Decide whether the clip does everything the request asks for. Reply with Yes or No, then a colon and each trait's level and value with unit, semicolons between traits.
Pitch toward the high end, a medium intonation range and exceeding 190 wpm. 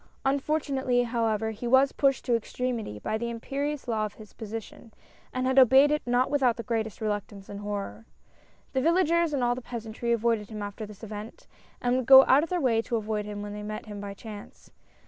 Yes: high, 235 Hz; average, 3.6 semitones; fast, 205 wpm